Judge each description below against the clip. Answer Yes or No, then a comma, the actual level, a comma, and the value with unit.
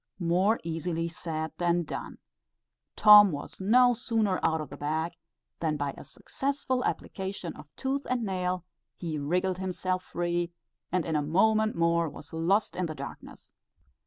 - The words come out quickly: No, average, 155 wpm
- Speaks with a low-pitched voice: No, medium, 175 Hz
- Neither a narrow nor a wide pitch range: Yes, average, 4.2 semitones